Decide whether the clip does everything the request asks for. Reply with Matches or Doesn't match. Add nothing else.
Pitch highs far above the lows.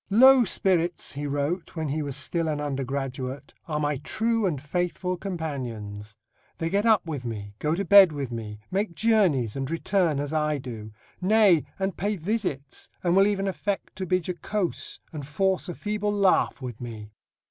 Matches